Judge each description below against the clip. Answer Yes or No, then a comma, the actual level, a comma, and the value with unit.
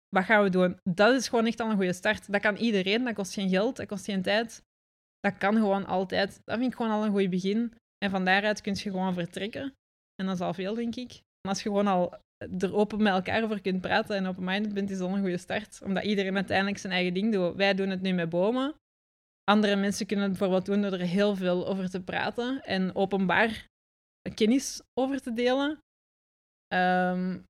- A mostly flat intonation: Yes, narrow, 2.3 semitones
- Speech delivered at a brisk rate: Yes, fast, 225 wpm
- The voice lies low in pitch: No, high, 200 Hz